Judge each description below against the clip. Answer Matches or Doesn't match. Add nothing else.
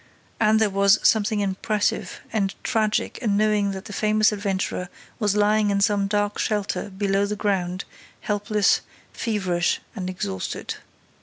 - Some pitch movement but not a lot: Doesn't match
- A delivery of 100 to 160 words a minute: Matches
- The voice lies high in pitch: Matches